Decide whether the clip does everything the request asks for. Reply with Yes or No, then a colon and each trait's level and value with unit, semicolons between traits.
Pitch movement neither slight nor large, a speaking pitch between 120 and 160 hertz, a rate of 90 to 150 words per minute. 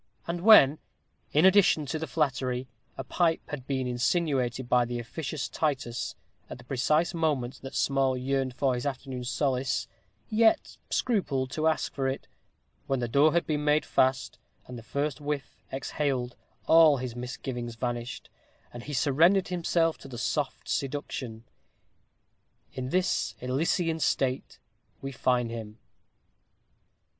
Yes: average, 3.7 semitones; low, 135 Hz; average, 140 wpm